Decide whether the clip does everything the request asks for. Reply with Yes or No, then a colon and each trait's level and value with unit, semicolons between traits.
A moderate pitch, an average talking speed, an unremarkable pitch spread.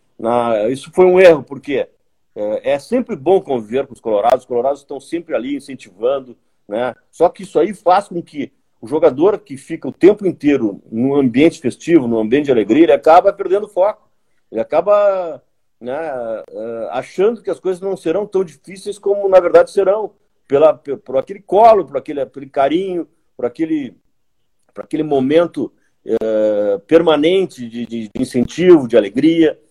No: medium, 175 Hz; average, 170 wpm; wide, 7.0 semitones